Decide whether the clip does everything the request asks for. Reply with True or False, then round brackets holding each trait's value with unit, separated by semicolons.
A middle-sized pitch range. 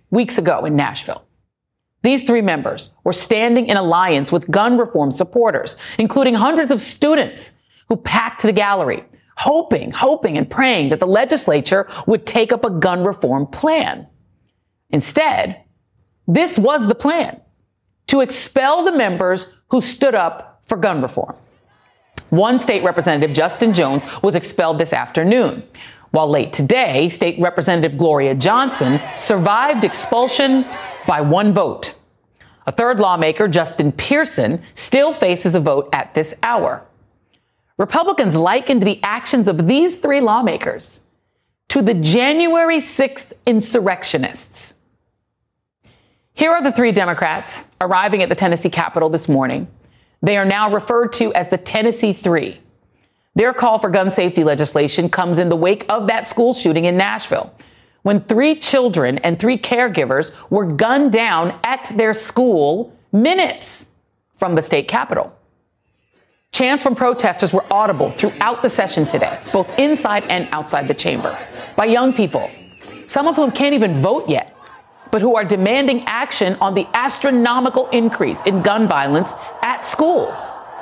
False (6.1 semitones)